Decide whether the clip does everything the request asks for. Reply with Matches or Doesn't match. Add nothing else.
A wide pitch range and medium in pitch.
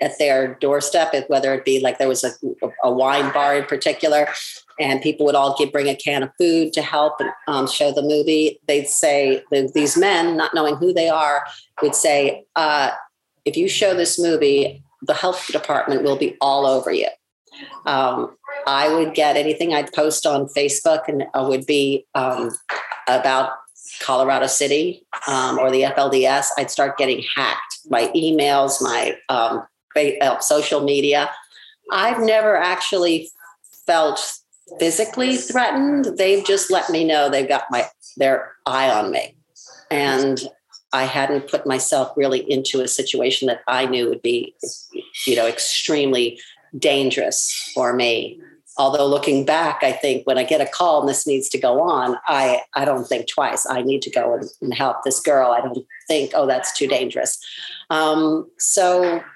Doesn't match